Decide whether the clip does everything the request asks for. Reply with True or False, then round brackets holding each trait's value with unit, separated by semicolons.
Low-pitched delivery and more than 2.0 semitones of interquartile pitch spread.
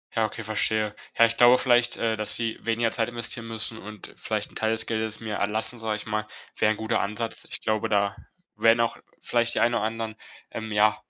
False (110 Hz; 1.3 semitones)